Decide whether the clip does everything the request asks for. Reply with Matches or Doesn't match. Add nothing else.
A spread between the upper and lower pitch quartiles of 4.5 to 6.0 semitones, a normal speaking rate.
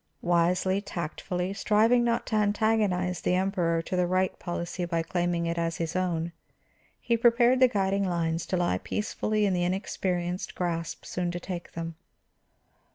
Doesn't match